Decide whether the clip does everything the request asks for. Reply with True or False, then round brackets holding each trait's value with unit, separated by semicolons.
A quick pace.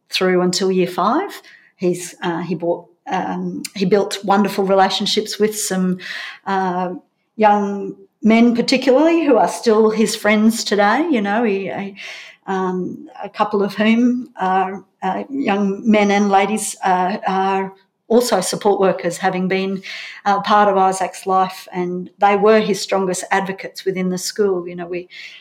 False (150 wpm)